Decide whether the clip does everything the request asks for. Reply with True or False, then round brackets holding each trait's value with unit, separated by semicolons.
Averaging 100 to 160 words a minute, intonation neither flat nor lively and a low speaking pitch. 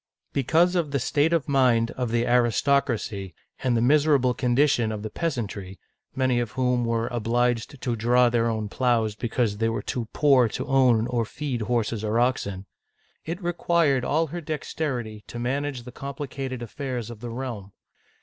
False (175 wpm; 3.3 semitones; 125 Hz)